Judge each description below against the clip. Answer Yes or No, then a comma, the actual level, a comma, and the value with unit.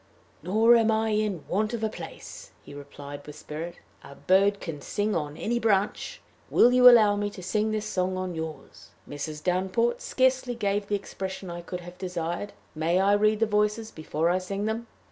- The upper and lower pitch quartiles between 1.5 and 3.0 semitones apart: No, average, 3.9 semitones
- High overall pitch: Yes, high, 200 Hz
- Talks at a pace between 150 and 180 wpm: No, average, 190 wpm